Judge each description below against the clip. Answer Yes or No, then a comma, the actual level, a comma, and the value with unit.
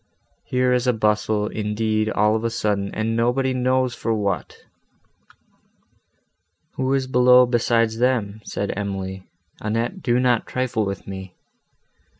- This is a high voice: No, low, 115 Hz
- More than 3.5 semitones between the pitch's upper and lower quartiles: No, average, 3.0 semitones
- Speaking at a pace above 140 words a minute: No, slow, 135 wpm